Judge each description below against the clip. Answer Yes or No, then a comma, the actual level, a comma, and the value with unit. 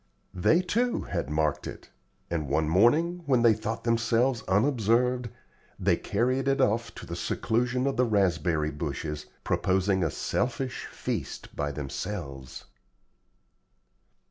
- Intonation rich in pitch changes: Yes, wide, 7.6 semitones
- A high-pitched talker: No, low, 110 Hz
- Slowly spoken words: Yes, slow, 125 wpm